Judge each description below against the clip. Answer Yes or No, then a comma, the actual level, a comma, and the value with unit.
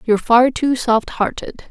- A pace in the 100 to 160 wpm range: Yes, average, 140 wpm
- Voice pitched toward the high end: Yes, high, 240 Hz